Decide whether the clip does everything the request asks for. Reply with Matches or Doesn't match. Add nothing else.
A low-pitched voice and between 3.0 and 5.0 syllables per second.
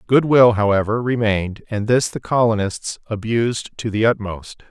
Matches